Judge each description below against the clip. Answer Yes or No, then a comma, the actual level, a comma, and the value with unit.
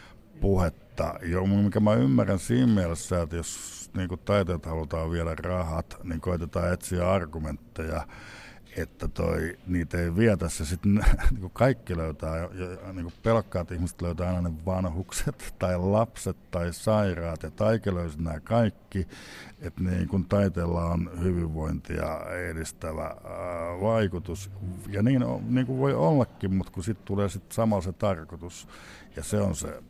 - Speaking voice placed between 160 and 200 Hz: No, very low, 90 Hz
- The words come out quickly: No, average, 135 wpm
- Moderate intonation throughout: Yes, average, 3.2 semitones